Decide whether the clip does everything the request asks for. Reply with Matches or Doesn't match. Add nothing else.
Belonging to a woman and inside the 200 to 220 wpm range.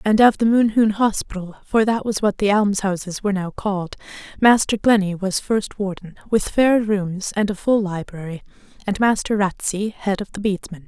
Doesn't match